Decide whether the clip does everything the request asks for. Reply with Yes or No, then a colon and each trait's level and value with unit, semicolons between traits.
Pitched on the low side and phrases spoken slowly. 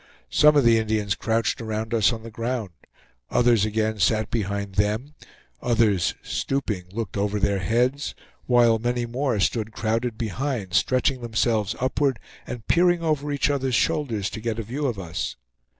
No: low, 115 Hz; average, 160 wpm